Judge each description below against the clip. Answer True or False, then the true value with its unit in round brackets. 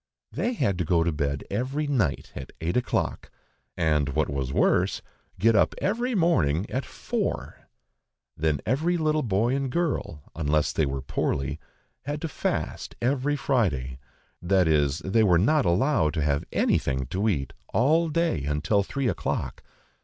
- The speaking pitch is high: False (95 Hz)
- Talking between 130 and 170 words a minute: True (155 wpm)